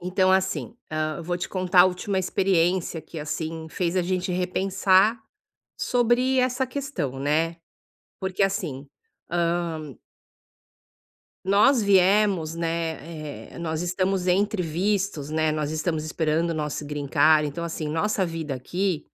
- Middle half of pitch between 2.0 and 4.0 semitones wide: Yes, average, 3.4 semitones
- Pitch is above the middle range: No, medium, 175 Hz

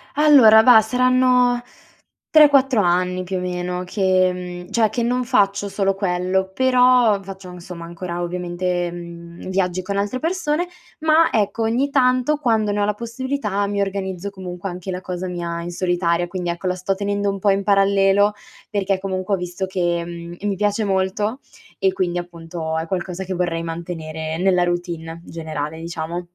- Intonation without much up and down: No, average, 3.0 semitones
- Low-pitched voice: No, high, 190 Hz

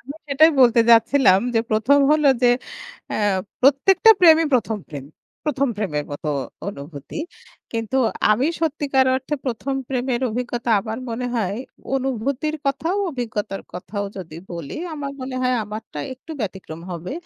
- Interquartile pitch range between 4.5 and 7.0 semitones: Yes, average, 5.0 semitones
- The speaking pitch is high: Yes, high, 245 Hz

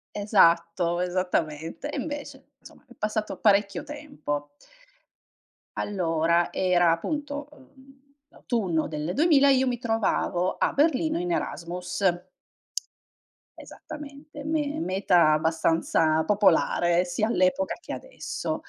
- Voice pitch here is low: No, high, 200 Hz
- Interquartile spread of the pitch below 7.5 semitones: No, wide, 8.8 semitones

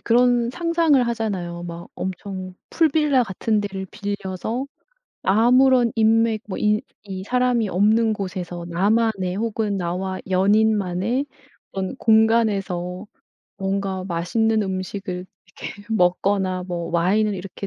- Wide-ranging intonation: No, average, 3.3 semitones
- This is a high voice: Yes, high, 205 Hz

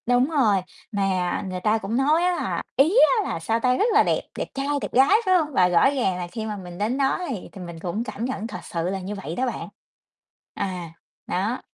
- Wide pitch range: Yes, wide, 6.4 semitones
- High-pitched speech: Yes, high, 215 Hz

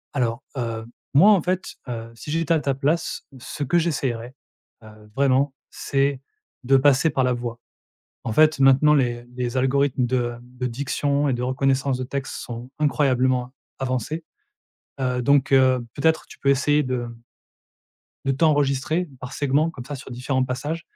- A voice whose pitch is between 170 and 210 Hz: No, low, 135 Hz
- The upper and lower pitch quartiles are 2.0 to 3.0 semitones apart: Yes, narrow, 2.5 semitones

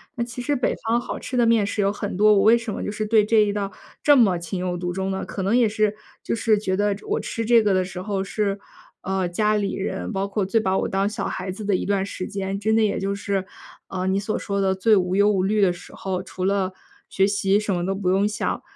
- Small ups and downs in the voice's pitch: Yes, narrow, 2.0 semitones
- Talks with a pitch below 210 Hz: Yes, high, 200 Hz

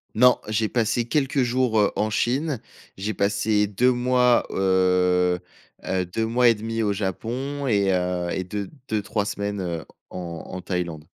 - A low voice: Yes, low, 105 Hz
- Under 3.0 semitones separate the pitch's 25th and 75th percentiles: No, average, 4.5 semitones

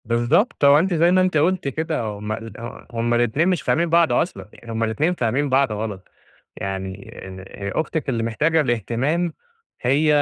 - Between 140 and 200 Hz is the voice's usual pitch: No, low, 130 Hz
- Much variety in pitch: Yes, wide, 6.2 semitones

